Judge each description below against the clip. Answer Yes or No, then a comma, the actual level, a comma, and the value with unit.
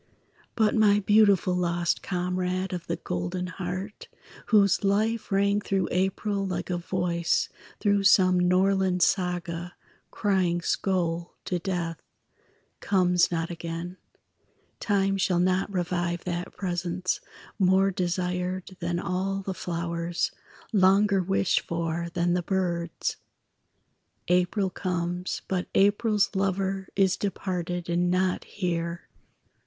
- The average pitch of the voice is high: No, medium, 180 Hz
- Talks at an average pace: No, slow, 115 wpm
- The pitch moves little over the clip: Yes, narrow, 1.8 semitones